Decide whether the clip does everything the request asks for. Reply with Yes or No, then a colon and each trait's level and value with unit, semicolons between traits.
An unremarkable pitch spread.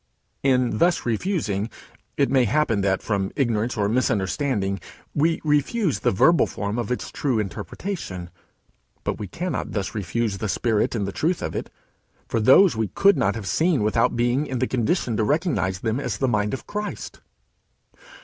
No: wide, 6.0 semitones